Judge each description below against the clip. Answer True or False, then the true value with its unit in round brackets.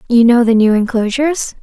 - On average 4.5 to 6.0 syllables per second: True (5.7 syllables/s)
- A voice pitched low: False (240 Hz)